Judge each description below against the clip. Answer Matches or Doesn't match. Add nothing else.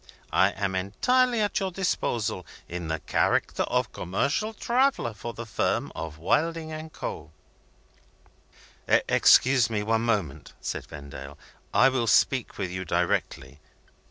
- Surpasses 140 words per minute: Doesn't match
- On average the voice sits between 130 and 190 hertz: Doesn't match